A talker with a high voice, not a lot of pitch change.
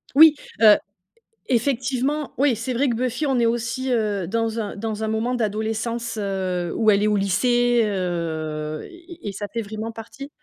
No: high, 225 Hz; average, 3.3 semitones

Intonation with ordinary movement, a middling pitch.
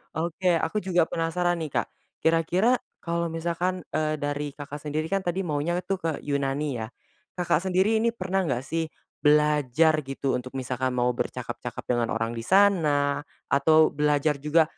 Yes: average, 3.6 semitones; medium, 155 Hz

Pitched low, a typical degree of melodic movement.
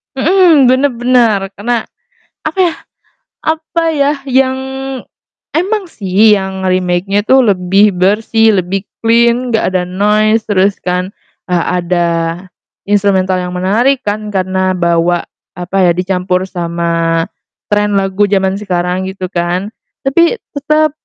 No: high, 200 Hz; average, 4.9 semitones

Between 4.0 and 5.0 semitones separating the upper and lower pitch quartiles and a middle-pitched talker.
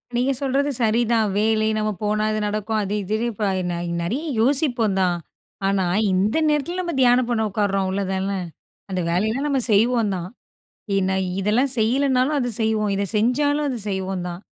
No: average, 4.4 semitones; high, 220 Hz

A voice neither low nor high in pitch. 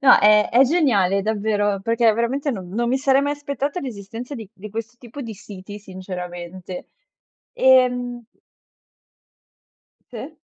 No: high, 230 Hz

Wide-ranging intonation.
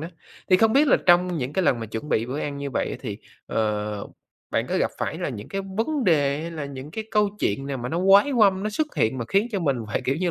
Yes: wide, 7.3 semitones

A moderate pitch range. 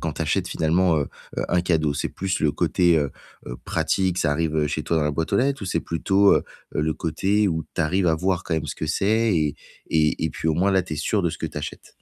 Yes: average, 3.3 semitones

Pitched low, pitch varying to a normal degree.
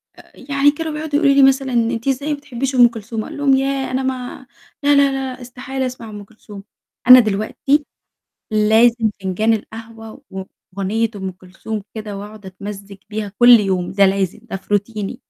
No: high, 230 Hz; average, 4.6 semitones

